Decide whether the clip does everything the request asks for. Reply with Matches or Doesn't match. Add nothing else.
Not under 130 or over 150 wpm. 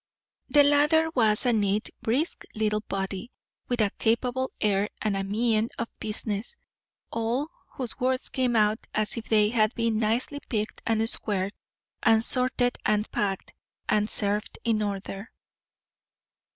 Matches